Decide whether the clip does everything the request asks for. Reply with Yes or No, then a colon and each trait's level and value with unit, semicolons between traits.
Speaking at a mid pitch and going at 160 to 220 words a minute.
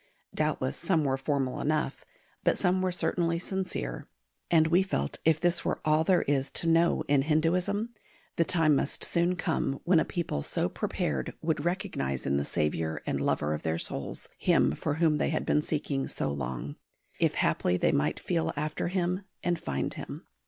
Yes: medium, 155 Hz; average, 180 wpm